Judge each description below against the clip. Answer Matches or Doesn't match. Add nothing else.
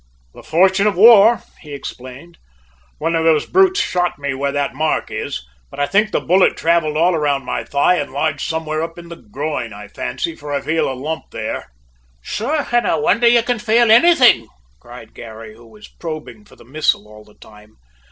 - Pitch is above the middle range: Doesn't match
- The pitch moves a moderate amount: Doesn't match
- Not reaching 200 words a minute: Matches